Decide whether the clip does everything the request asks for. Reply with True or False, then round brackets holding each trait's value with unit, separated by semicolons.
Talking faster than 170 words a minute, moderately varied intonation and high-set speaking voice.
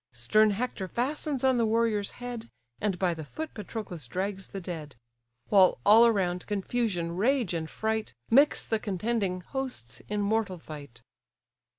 False (150 wpm; 4.6 semitones; 205 Hz)